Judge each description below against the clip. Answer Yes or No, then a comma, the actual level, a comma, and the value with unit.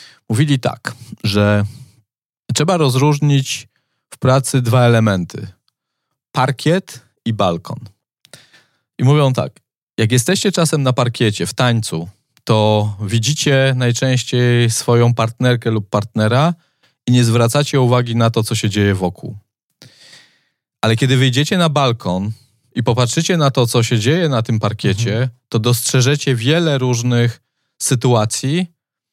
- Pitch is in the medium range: No, low, 125 Hz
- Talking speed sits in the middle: Yes, average, 120 wpm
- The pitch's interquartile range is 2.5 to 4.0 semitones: Yes, average, 3.2 semitones